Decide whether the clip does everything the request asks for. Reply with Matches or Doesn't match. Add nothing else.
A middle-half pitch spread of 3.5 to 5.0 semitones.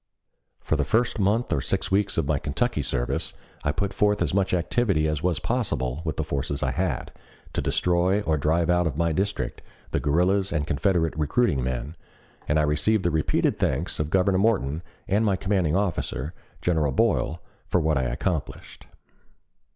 Matches